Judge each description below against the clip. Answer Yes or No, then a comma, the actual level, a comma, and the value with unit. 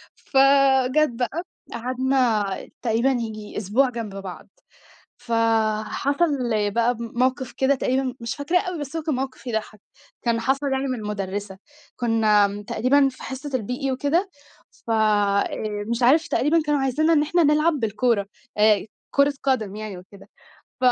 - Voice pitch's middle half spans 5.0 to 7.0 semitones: No, average, 4.1 semitones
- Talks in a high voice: Yes, very high, 250 Hz